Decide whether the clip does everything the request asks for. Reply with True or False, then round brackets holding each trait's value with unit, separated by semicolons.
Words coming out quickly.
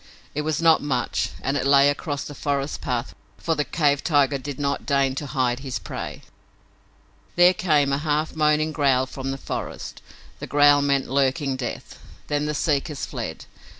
False (175 wpm)